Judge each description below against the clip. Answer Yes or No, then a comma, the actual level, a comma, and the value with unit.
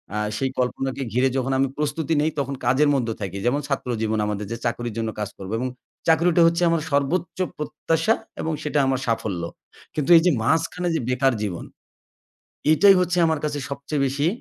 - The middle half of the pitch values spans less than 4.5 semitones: No, average, 4.8 semitones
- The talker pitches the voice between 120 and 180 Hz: Yes, medium, 140 Hz